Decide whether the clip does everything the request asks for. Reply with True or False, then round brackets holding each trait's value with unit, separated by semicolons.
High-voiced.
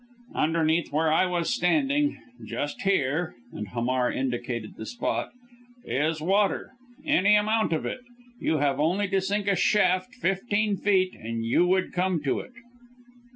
False (180 Hz)